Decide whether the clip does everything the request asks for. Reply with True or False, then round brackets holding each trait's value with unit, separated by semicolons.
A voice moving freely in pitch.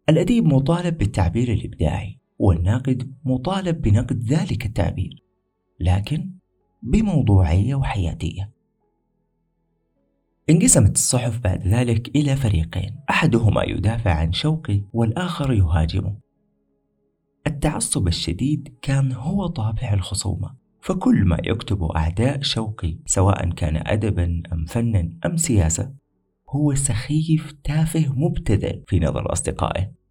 True (7.5 semitones)